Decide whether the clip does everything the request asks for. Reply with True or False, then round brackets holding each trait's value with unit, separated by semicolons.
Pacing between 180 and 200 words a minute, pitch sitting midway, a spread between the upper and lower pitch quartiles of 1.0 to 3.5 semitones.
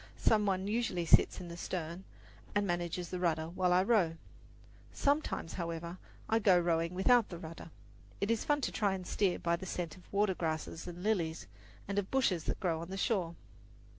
True (190 wpm; 180 Hz; 3.1 semitones)